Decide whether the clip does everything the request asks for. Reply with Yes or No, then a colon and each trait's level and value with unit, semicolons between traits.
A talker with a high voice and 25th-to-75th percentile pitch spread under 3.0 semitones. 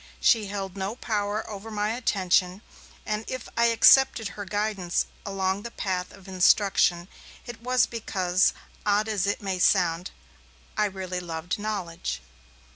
Yes: high, 200 Hz; narrow, 2.6 semitones